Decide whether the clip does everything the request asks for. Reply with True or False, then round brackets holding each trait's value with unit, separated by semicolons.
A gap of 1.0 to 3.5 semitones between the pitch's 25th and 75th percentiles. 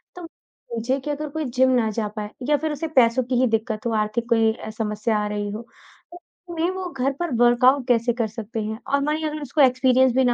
False (4.0 semitones)